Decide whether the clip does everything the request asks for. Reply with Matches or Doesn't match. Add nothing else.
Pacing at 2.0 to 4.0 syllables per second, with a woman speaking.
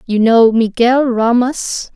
Matches